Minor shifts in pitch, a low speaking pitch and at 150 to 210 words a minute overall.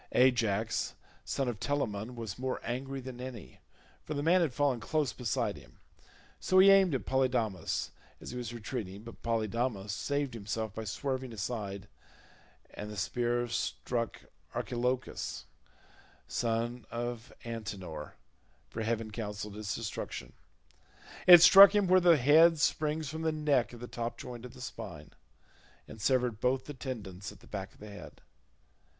No: average, 3.7 semitones; low, 120 Hz; average, 155 wpm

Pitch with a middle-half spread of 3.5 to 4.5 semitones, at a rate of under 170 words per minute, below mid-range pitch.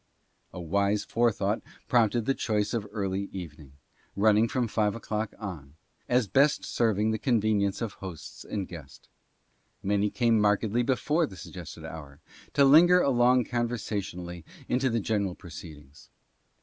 Yes: average, 3.8 semitones; average, 150 wpm; low, 105 Hz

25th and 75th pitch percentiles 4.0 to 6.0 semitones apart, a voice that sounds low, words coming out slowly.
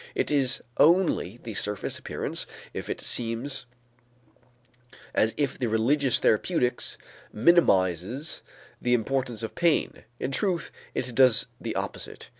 Yes: average, 4.3 semitones; low, 125 Hz; slow, 120 wpm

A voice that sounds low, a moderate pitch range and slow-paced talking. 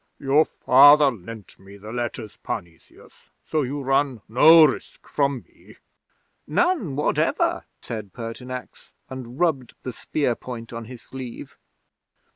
Yes: low, 125 Hz; average, 3.8 semitones; slow, 125 wpm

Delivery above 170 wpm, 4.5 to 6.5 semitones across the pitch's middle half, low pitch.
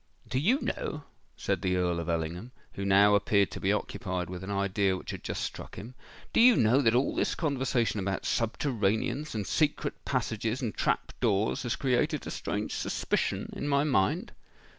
Yes: average, 180 wpm; wide, 5.5 semitones; low, 110 Hz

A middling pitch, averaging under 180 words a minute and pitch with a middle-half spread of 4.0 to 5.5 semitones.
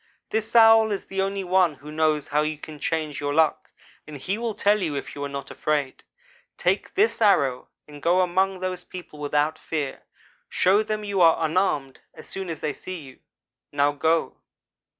No: medium, 165 Hz; average, 190 wpm; average, 4.7 semitones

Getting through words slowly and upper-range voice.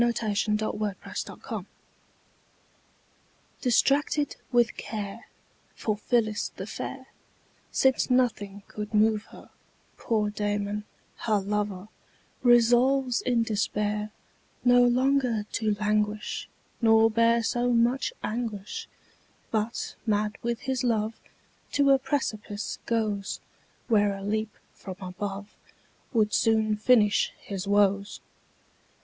Yes: slow, 105 wpm; high, 215 Hz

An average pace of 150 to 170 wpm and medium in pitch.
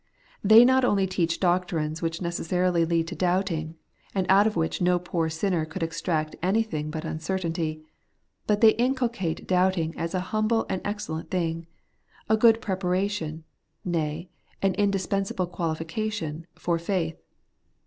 No: average, 140 wpm; medium, 180 Hz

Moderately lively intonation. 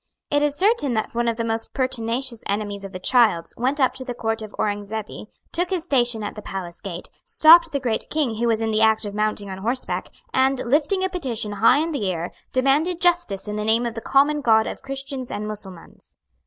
Yes: average, 4.5 semitones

